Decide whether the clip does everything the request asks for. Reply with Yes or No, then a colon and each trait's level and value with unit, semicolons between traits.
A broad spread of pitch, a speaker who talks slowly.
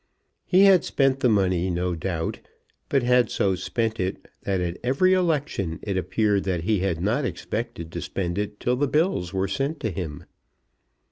No: wide, 6.3 semitones; average, 180 wpm